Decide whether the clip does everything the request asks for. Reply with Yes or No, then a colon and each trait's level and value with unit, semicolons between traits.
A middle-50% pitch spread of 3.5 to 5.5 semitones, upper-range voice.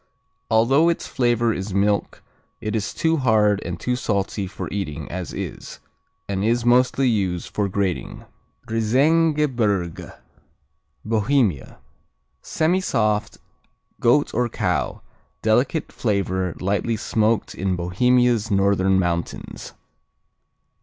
No: average, 4.1 semitones; low, 110 Hz